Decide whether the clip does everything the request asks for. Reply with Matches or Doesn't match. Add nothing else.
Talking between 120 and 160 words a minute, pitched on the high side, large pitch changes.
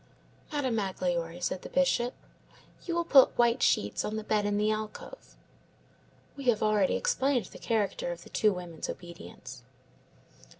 Matches